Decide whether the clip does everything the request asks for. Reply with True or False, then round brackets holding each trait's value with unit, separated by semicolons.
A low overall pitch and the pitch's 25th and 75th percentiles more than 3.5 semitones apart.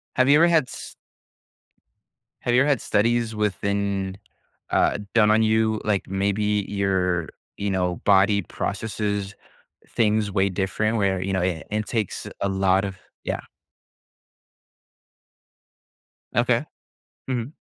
False (100 Hz; 2.4 semitones)